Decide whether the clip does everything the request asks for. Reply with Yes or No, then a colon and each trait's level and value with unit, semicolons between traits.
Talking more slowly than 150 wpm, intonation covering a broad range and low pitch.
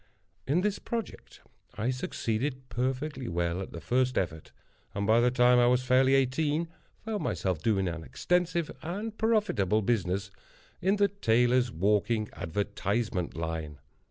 Yes: average, 140 wpm; wide, 7.2 semitones; low, 120 Hz